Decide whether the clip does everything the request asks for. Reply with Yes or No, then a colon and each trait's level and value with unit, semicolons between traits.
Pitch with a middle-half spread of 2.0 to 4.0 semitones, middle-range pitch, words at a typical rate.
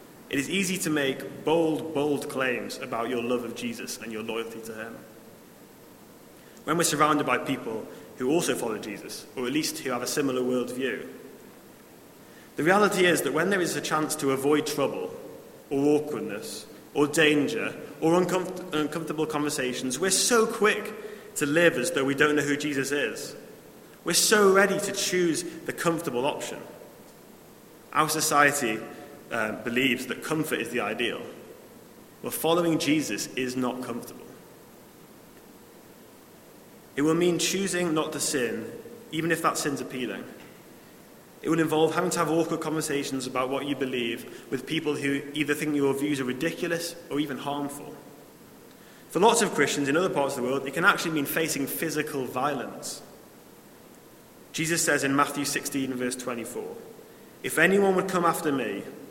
Yes: average, 3.5 semitones; medium, 150 Hz; average, 160 wpm